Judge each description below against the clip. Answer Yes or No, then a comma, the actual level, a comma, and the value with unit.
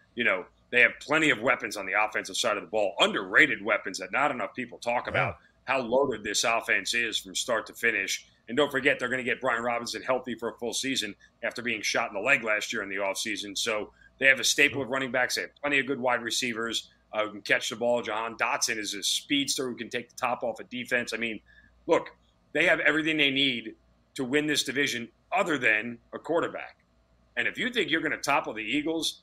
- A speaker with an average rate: No, fast, 240 wpm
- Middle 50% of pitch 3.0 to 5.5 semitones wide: Yes, average, 3.7 semitones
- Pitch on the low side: Yes, low, 120 Hz